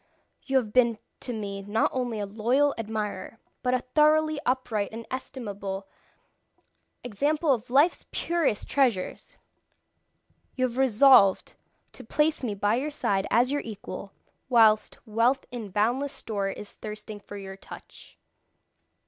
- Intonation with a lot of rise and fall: No, average, 4.3 semitones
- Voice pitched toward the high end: Yes, high, 230 Hz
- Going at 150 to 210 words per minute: No, slow, 135 wpm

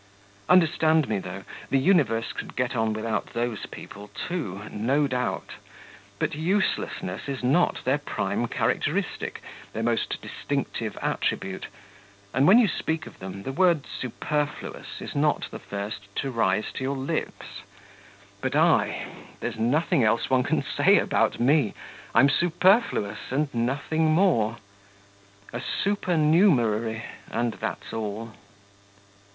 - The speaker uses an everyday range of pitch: No, wide, 5.8 semitones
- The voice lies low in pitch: Yes, low, 130 Hz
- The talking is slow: Yes, slow, 130 wpm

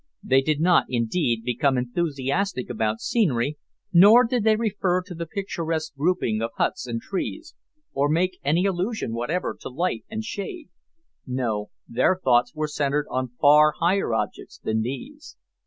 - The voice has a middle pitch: Yes, medium, 150 Hz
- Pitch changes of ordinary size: No, wide, 6.9 semitones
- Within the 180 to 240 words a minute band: No, average, 155 wpm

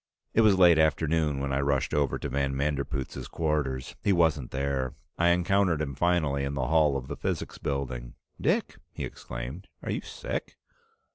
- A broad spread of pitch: No, average, 3.2 semitones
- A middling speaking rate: Yes, average, 170 wpm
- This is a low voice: Yes, very low, 70 Hz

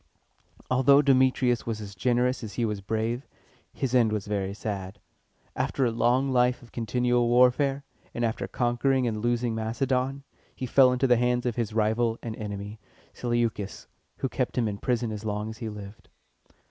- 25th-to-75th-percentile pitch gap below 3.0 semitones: Yes, narrow, 2.6 semitones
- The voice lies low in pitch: Yes, low, 120 Hz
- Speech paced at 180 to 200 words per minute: No, average, 170 wpm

